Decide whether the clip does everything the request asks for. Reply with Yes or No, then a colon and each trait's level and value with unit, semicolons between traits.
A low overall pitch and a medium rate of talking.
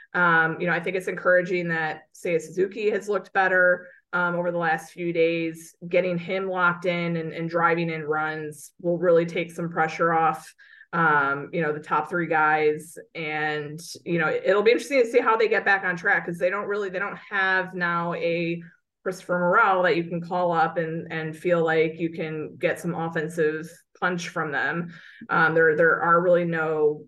No: medium, 170 Hz; average, 195 wpm